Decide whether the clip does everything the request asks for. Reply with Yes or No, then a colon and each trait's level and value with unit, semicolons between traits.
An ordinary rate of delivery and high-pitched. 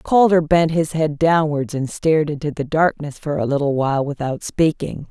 No: average, 190 wpm; medium, 150 Hz